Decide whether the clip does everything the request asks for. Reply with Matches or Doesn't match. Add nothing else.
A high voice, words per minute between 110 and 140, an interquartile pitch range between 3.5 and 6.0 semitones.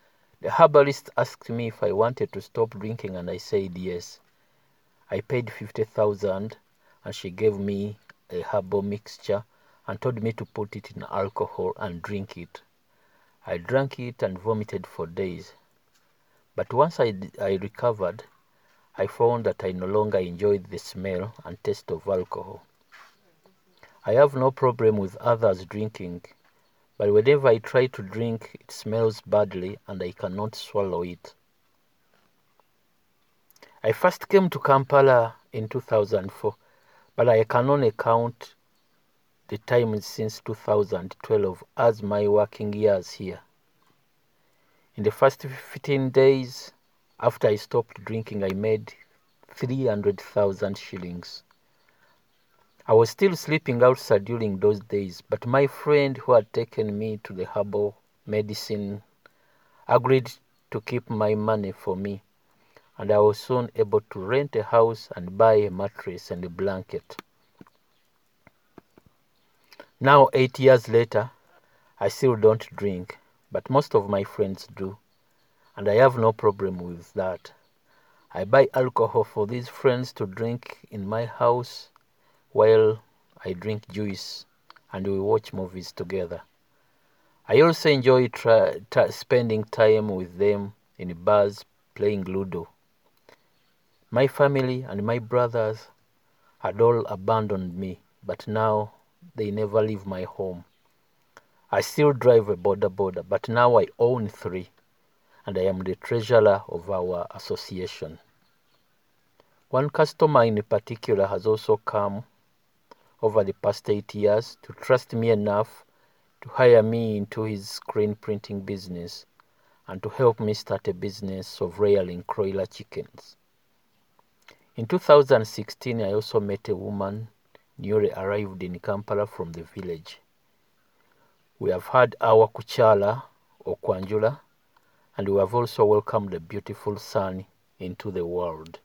Doesn't match